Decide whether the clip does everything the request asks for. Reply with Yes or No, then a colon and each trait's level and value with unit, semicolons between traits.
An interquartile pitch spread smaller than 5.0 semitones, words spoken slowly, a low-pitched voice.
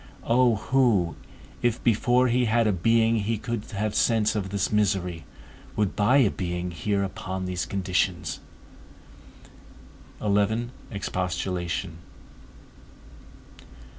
Yes: average, 3.8 semitones; slow, 105 wpm; low, 105 Hz